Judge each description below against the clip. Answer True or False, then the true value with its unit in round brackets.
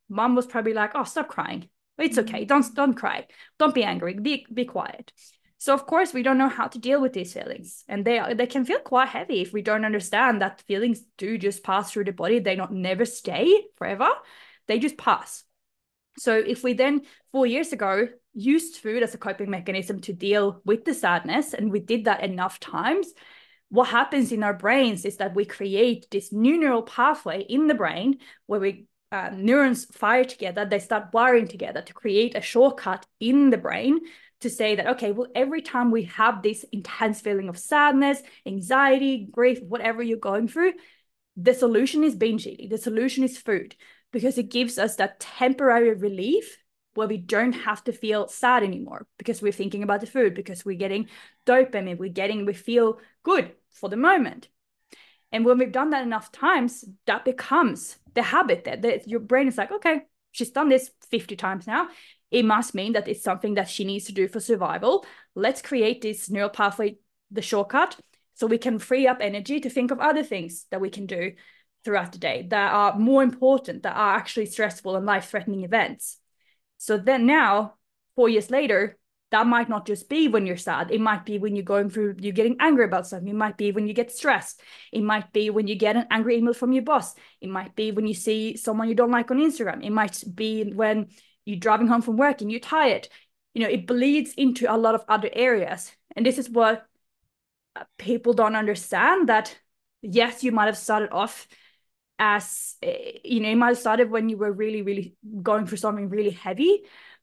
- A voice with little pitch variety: False (3.9 semitones)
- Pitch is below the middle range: False (225 Hz)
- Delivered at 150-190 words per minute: False (200 wpm)